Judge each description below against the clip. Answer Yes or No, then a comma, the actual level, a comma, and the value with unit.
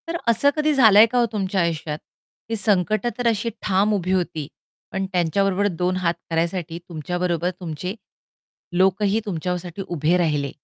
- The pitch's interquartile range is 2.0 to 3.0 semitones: No, average, 3.5 semitones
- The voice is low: No, medium, 185 Hz